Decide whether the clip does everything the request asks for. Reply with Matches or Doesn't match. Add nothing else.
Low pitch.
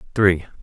Matches